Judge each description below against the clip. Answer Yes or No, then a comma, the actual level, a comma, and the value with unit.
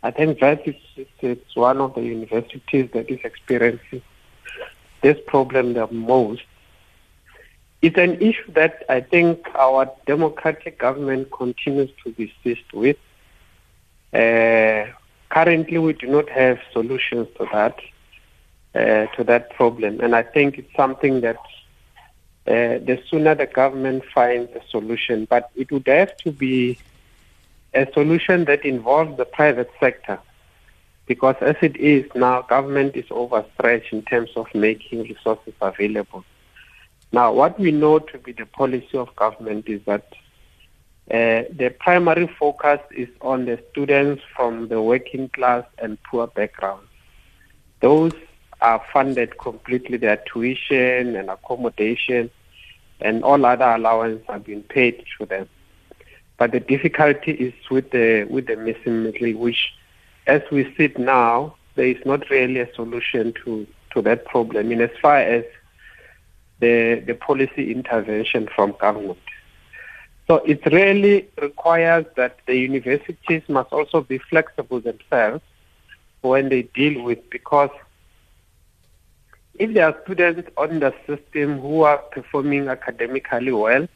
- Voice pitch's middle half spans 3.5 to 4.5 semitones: Yes, average, 4.0 semitones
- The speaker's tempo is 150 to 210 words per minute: No, average, 140 wpm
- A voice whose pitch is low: Yes, low, 125 Hz